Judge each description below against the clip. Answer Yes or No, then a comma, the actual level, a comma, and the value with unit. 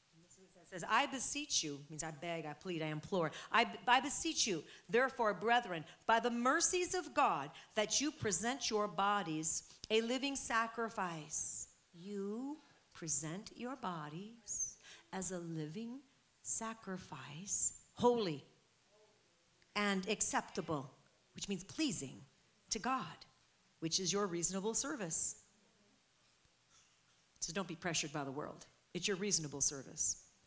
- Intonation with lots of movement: Yes, wide, 6.0 semitones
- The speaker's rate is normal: No, slow, 125 wpm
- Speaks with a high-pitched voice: Yes, high, 195 Hz